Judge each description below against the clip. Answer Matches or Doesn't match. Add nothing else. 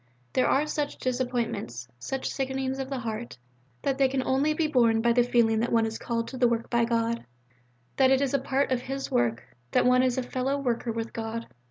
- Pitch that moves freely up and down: Doesn't match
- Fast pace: Matches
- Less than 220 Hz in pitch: Doesn't match